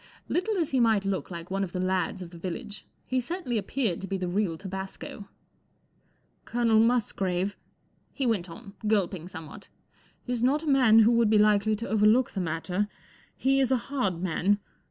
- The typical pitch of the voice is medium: No, high, 210 Hz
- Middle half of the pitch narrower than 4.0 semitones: No, average, 4.3 semitones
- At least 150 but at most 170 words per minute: No, average, 185 wpm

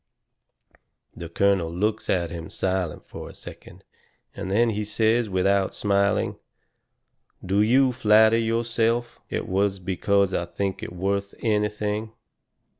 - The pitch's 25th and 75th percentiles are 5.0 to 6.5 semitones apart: No, average, 2.7 semitones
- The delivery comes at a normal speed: No, slow, 125 wpm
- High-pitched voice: No, low, 100 Hz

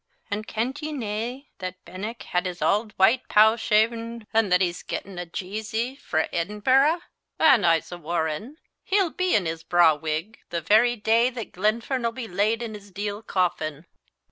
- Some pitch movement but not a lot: Yes, average, 4.7 semitones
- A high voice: Yes, high, 210 Hz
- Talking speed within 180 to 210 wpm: No, average, 170 wpm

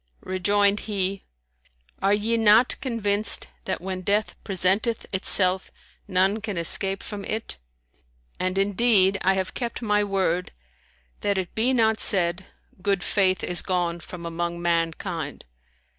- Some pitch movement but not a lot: No, narrow, 2.3 semitones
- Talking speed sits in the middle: No, slow, 130 wpm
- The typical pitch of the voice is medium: No, high, 195 Hz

